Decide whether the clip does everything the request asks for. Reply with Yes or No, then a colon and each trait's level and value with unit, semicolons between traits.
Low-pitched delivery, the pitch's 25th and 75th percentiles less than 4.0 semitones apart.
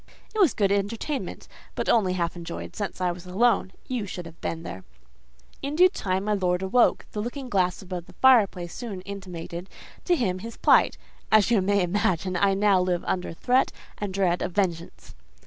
No: high, 195 Hz; average, 3.3 semitones